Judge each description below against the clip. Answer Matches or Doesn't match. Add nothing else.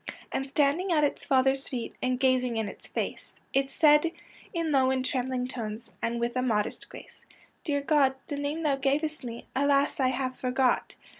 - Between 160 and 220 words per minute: Matches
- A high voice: Matches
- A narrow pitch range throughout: Matches